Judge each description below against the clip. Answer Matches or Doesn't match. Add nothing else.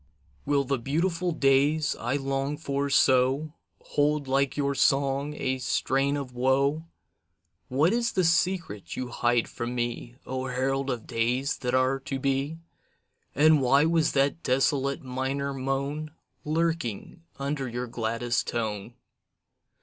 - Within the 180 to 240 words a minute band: Doesn't match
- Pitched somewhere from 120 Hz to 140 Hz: Matches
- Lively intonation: Doesn't match